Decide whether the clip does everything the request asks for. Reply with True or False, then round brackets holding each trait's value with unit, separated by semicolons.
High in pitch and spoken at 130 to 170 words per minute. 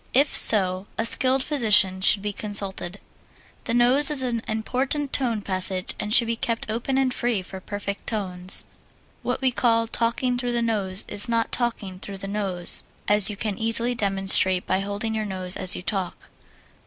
False (215 Hz; 180 wpm)